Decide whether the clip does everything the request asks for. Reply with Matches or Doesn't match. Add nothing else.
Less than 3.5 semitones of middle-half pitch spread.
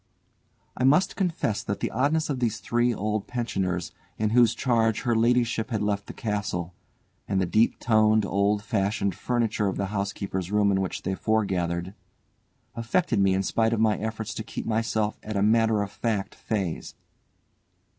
Matches